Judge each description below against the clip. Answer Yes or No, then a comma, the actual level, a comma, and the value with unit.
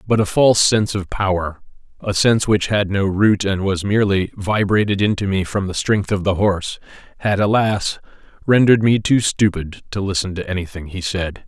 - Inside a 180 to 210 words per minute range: Yes, average, 190 wpm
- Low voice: Yes, low, 100 Hz